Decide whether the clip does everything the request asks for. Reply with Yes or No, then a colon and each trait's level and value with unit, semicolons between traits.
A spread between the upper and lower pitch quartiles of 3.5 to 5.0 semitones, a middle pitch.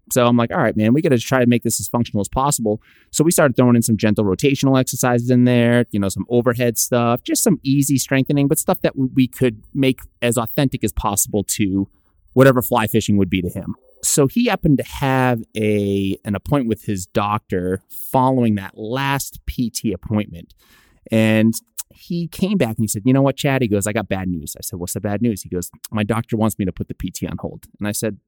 No: average, 4.0 semitones; low, 115 Hz